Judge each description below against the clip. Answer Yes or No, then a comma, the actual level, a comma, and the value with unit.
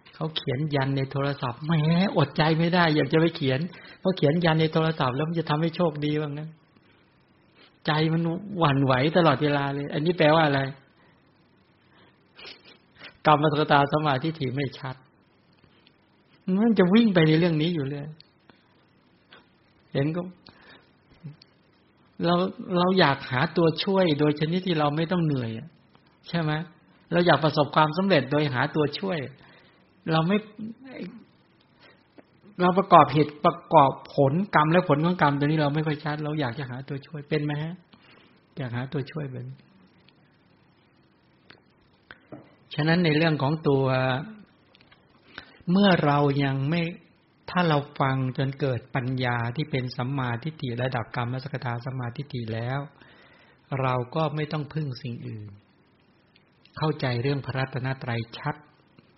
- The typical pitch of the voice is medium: Yes, medium, 150 Hz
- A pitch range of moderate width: Yes, average, 3.4 semitones